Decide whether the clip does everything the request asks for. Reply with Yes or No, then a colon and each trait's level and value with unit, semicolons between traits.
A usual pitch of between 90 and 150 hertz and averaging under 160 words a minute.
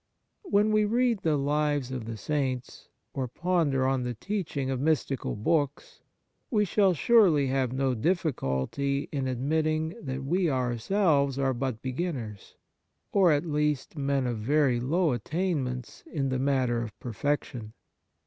Yes: medium, 140 Hz; average, 150 wpm